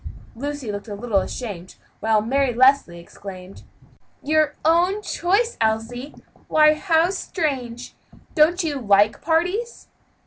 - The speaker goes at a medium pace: No, slow, 115 wpm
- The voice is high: Yes, very high, 275 Hz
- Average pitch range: No, wide, 6.8 semitones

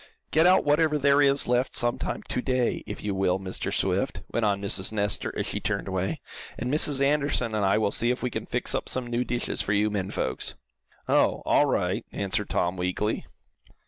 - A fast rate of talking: Yes, fast, 210 wpm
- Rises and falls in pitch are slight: No, average, 5.2 semitones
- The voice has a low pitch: Yes, low, 115 Hz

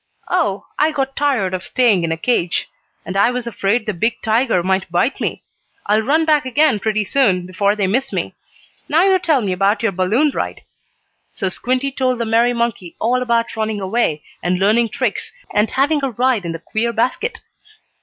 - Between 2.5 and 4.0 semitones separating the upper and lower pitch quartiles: No, average, 4.9 semitones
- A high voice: Yes, high, 230 Hz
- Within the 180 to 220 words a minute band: Yes, average, 195 wpm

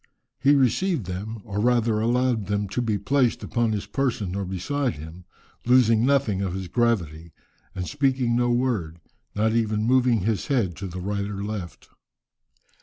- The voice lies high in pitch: No, low, 110 Hz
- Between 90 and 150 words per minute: No, average, 165 wpm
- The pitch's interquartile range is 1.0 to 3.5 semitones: No, average, 4.1 semitones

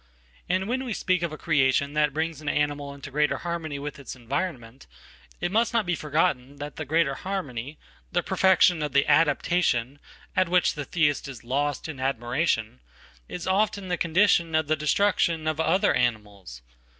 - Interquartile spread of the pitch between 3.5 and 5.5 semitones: Yes, average, 4.2 semitones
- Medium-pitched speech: Yes, medium, 150 Hz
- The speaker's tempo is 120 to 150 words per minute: No, average, 160 wpm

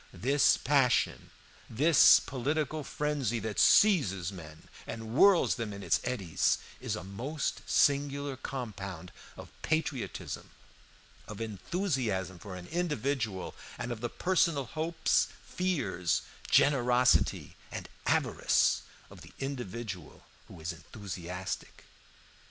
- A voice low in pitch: Yes, low, 120 Hz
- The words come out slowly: Yes, slow, 110 wpm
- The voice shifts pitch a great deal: Yes, wide, 6.8 semitones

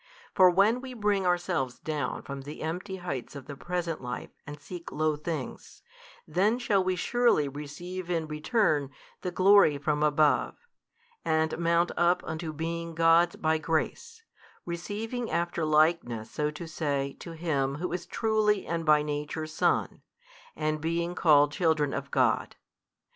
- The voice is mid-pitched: Yes, medium, 165 Hz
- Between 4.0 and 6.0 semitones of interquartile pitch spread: No, average, 3.2 semitones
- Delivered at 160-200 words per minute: No, average, 150 wpm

